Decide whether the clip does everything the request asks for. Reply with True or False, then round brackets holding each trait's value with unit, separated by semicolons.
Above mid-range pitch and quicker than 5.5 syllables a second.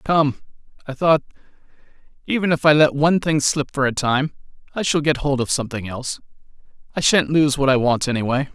False (140 Hz; 5.9 syllables/s)